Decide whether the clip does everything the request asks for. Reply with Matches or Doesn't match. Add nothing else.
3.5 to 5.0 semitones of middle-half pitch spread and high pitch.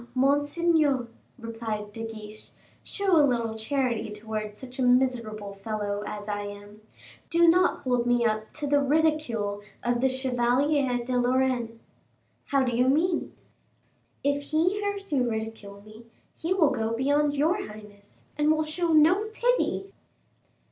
Doesn't match